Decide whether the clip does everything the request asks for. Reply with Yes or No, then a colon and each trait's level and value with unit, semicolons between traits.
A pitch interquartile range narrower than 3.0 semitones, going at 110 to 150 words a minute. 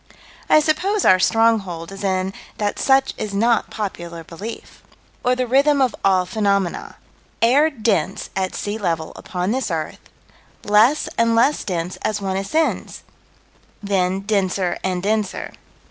No: average, 3.9 semitones; average, 140 wpm